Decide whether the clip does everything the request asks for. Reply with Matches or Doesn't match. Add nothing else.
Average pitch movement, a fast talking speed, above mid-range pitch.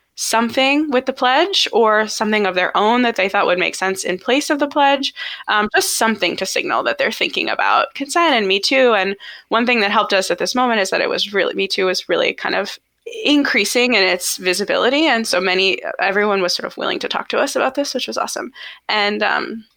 Doesn't match